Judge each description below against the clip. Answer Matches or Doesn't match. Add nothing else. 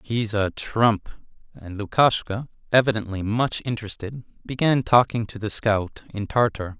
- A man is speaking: Matches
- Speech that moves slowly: Matches